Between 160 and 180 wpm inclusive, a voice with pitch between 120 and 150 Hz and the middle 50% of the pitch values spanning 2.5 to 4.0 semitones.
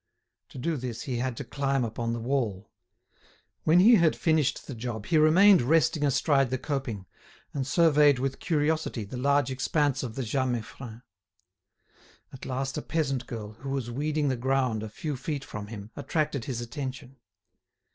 Yes: average, 170 wpm; low, 135 Hz; average, 3.6 semitones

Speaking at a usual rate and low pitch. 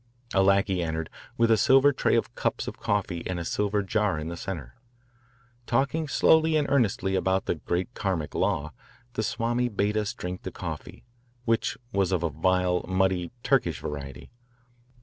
Yes: average, 170 wpm; very low, 95 Hz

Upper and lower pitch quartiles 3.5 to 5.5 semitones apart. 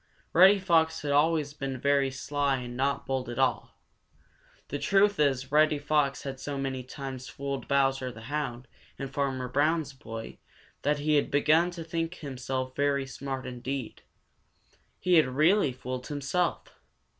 No: narrow, 2.5 semitones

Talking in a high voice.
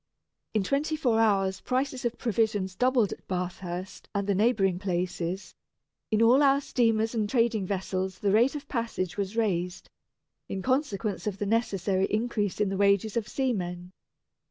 Yes: high, 210 Hz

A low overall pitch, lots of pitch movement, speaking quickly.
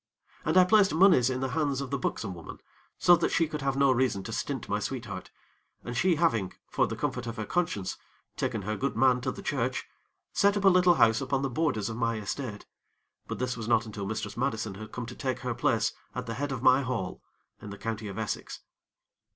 No: low, 125 Hz; average, 4.1 semitones; fast, 225 wpm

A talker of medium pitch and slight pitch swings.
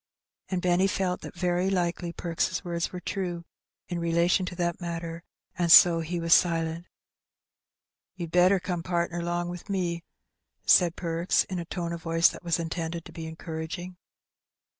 Yes: medium, 170 Hz; narrow, 1.1 semitones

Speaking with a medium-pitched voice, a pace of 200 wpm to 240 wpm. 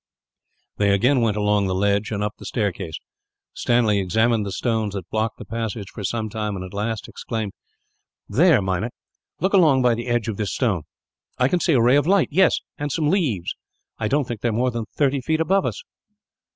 No: low, 115 Hz; fast, 205 wpm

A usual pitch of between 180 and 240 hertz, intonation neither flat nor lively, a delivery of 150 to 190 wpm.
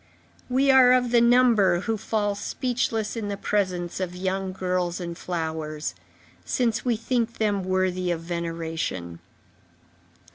No: high, 190 Hz; average, 4.8 semitones; slow, 135 wpm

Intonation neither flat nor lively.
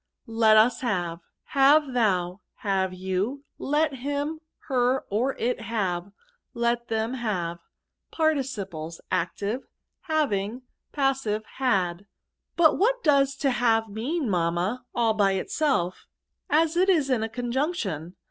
No: wide, 6.1 semitones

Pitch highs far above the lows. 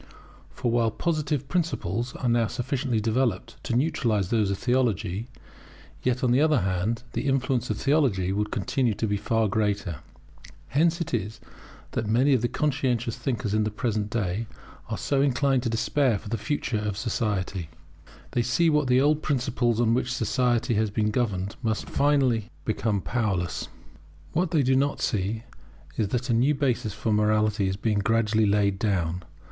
No: average, 3.7 semitones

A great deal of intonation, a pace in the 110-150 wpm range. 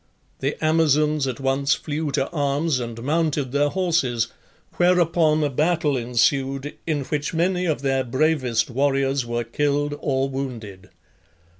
No: average, 2.8 semitones; slow, 135 wpm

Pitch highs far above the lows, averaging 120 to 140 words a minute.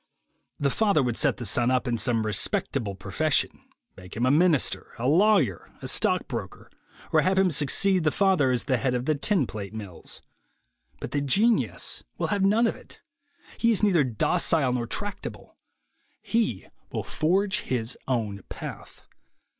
No: wide, 8.4 semitones; average, 160 wpm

